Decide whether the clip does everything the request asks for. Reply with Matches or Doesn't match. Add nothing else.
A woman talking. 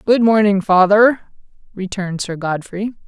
Matches